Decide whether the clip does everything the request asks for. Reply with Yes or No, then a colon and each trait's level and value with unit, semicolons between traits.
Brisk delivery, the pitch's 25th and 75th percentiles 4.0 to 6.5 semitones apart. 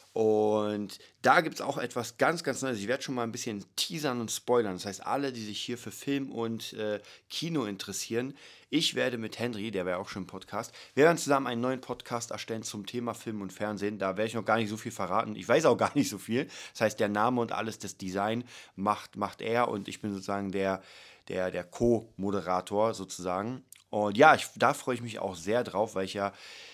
No: fast, 230 wpm; average, 3.3 semitones